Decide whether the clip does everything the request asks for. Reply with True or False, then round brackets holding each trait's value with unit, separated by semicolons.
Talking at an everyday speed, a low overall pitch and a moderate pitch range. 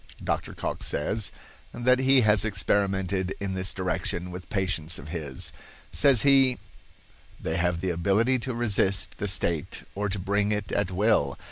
True (155 wpm; 100 Hz; 3.2 semitones)